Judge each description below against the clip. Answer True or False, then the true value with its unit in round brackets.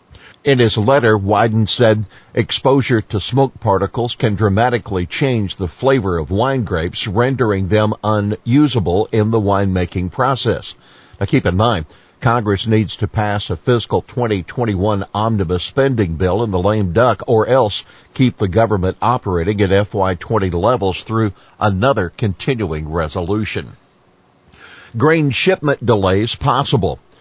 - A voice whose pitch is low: True (105 Hz)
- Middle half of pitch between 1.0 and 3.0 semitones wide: False (3.7 semitones)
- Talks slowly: True (130 wpm)